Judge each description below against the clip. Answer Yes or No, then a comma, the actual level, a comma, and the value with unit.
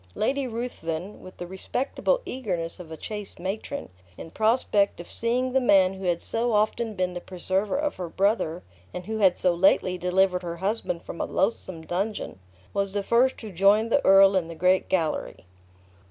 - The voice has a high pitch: Yes, high, 195 Hz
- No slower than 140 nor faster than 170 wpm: No, average, 185 wpm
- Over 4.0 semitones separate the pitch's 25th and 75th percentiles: No, average, 3.6 semitones